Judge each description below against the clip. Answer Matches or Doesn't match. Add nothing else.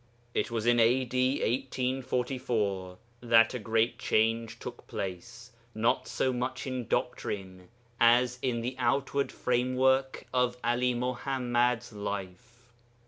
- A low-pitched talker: Matches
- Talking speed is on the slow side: Matches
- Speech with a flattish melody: Matches